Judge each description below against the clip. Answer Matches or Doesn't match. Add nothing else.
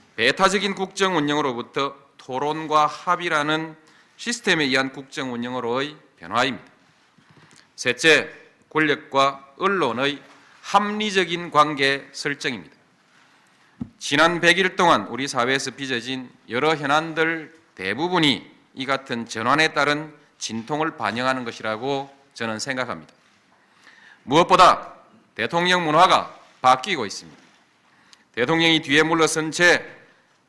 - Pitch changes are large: Doesn't match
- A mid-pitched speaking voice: Matches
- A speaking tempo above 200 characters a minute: Matches